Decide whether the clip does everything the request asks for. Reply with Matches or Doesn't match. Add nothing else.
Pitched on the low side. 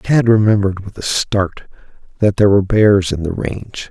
Matches